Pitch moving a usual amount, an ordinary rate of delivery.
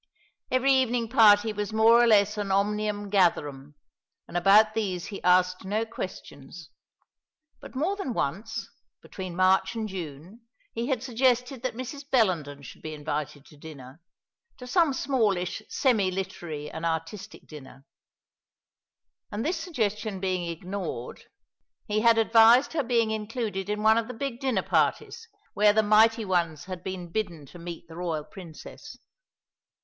Yes: average, 4.8 semitones; average, 150 wpm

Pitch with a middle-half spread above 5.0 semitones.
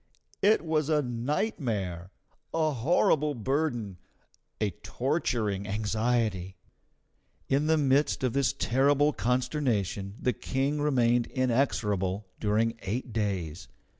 Yes: wide, 5.6 semitones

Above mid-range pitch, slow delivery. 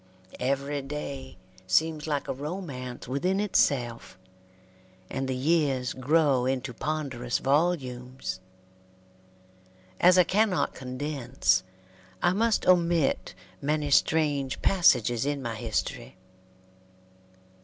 No: medium, 140 Hz; slow, 95 wpm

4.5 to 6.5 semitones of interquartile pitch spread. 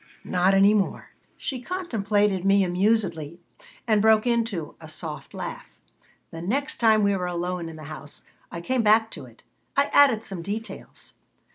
No: average, 4.1 semitones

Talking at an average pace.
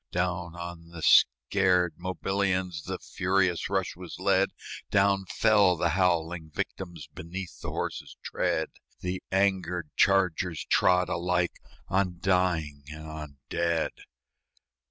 No: slow, 115 wpm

